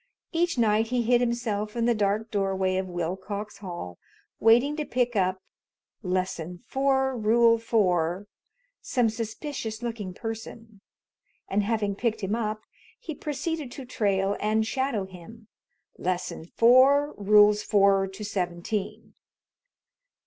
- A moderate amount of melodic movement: Yes, average, 3.5 semitones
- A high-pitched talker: Yes, high, 215 Hz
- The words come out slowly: Yes, slow, 125 wpm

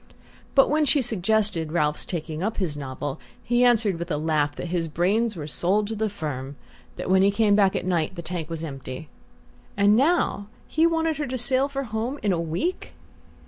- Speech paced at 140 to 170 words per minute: No, average, 195 wpm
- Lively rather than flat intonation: Yes, wide, 6.6 semitones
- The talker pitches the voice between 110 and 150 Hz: No, high, 195 Hz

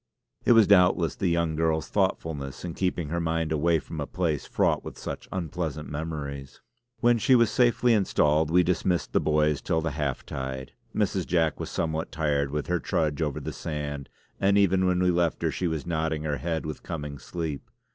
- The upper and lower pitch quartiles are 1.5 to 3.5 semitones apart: Yes, average, 3.1 semitones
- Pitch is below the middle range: Yes, very low, 80 Hz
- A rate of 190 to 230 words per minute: Yes, average, 195 wpm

